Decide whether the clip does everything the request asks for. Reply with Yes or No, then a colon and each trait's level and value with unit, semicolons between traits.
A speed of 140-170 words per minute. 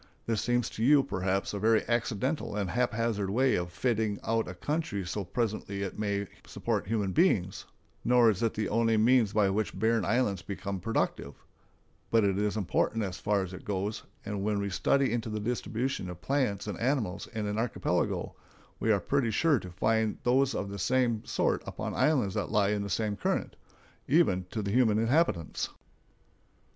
No: average, 185 wpm